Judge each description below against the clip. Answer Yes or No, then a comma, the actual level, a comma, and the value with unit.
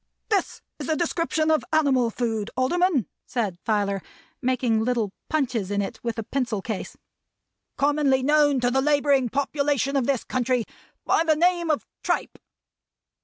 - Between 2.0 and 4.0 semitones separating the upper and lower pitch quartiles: No, average, 4.4 semitones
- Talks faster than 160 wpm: No, average, 150 wpm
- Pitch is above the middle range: Yes, very high, 265 Hz